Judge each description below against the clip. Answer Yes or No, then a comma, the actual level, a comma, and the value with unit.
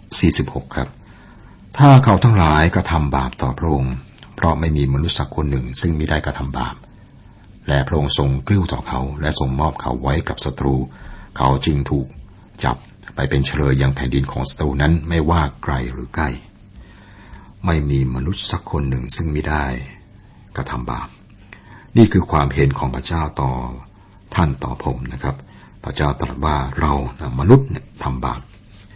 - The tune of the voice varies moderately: No, wide, 5.7 semitones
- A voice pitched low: Yes, very low, 75 Hz